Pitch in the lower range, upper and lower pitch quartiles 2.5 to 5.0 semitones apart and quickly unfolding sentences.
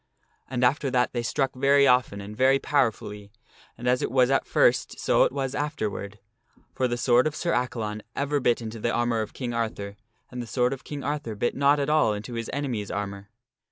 Yes: low, 125 Hz; average, 3.8 semitones; fast, 210 wpm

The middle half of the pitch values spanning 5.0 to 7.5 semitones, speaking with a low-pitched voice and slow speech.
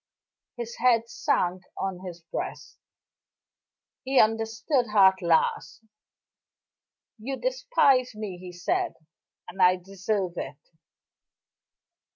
No: average, 5.3 semitones; high, 215 Hz; slow, 100 wpm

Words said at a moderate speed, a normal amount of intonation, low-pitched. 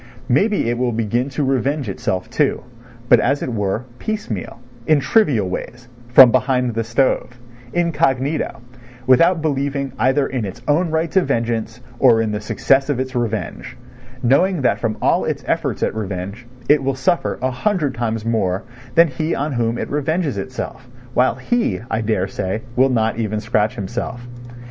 Yes: average, 165 wpm; average, 4.1 semitones; low, 125 Hz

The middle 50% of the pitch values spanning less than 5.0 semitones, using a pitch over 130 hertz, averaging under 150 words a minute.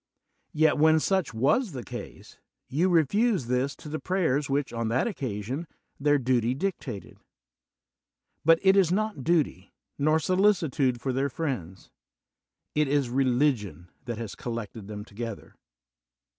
No: wide, 5.4 semitones; medium, 140 Hz; average, 140 wpm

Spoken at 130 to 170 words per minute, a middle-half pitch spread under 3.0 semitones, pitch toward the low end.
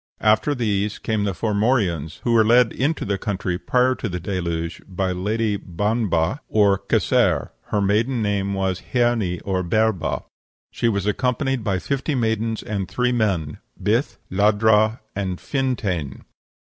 No: average, 150 wpm; average, 3.6 semitones; low, 105 Hz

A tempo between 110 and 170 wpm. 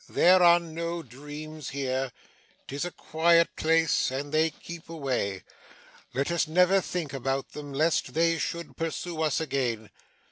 Yes: average, 145 wpm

